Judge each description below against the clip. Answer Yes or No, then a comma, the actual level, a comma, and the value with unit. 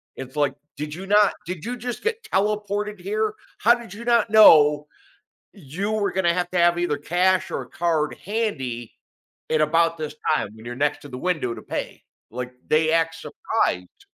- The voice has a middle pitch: Yes, medium, 175 Hz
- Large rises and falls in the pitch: Yes, wide, 5.9 semitones